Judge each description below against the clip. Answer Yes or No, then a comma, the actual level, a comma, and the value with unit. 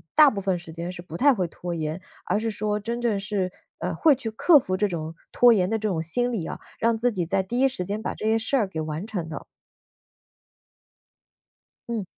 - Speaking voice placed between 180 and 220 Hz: Yes, high, 205 Hz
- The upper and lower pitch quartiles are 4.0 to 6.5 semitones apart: Yes, average, 4.6 semitones